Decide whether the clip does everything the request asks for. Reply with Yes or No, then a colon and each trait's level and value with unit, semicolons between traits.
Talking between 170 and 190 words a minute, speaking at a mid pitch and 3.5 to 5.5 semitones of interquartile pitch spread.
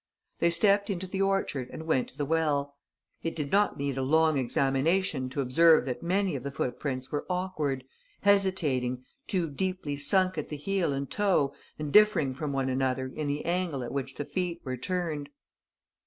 Yes: average, 185 wpm; medium, 150 Hz; average, 5.2 semitones